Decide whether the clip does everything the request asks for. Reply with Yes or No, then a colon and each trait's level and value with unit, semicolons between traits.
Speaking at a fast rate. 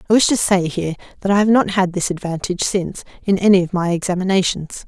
Yes: fast, 220 wpm